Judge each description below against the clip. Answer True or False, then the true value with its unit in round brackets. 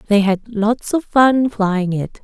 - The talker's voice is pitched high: True (215 Hz)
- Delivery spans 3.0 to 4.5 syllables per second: True (3.5 syllables/s)